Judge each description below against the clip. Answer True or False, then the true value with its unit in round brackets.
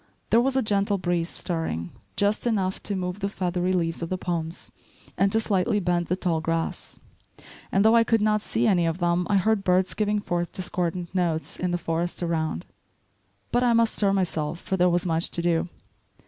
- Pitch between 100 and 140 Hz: False (180 Hz)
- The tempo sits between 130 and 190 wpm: False (200 wpm)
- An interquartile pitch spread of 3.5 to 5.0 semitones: False (3.0 semitones)